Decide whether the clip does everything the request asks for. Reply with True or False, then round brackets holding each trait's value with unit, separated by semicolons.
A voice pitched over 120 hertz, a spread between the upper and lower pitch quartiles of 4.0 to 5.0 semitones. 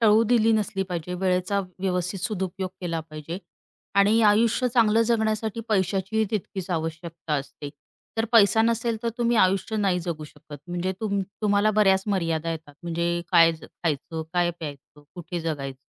True (185 Hz; 4.4 semitones)